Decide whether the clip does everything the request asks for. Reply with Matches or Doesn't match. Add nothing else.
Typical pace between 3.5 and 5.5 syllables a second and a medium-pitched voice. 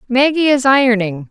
Doesn't match